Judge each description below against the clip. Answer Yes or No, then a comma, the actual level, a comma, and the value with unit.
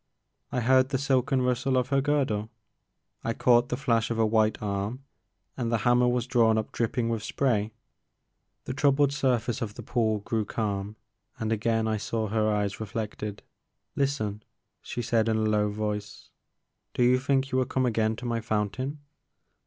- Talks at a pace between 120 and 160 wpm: No, average, 175 wpm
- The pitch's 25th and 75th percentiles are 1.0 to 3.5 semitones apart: Yes, average, 2.9 semitones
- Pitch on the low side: Yes, low, 115 Hz